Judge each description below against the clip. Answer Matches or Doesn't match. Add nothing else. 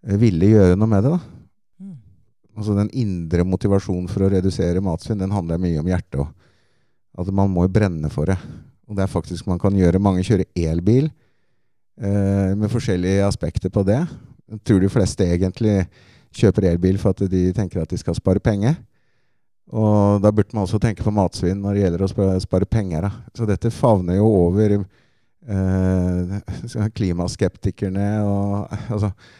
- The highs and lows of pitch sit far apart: Doesn't match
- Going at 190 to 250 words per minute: Doesn't match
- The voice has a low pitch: Matches